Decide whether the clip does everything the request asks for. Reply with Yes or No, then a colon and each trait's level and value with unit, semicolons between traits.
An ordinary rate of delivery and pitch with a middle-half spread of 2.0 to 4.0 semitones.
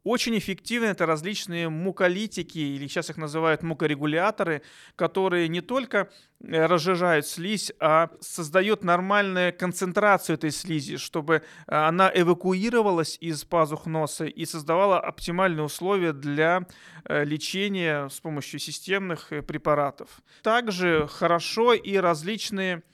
No: slow, 105 wpm; average, 3.3 semitones